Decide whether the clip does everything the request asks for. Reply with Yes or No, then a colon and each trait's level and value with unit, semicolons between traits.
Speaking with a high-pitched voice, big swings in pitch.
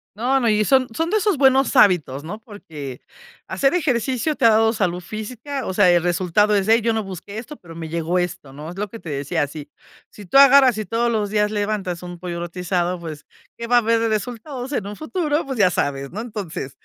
Yes: high, 210 Hz; wide, 5.7 semitones